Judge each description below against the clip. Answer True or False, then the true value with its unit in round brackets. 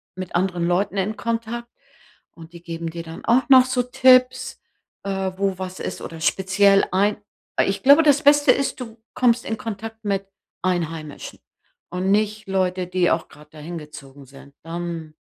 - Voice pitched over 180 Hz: True (190 Hz)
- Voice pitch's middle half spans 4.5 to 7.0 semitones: True (4.9 semitones)